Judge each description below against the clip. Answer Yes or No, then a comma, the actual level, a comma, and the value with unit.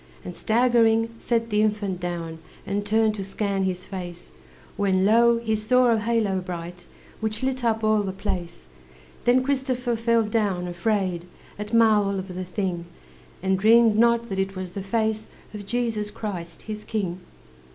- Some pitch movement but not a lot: Yes, average, 3.4 semitones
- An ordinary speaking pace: Yes, average, 160 wpm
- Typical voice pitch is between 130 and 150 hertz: No, high, 210 Hz